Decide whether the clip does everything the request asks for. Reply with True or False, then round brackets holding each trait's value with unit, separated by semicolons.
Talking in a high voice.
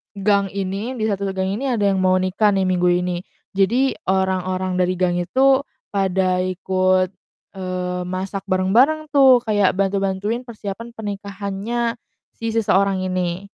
True (195 Hz)